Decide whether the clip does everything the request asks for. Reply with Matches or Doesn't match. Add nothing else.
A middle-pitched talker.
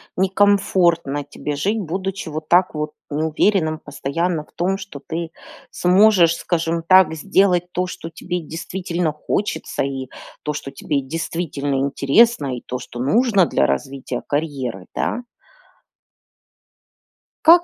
Matches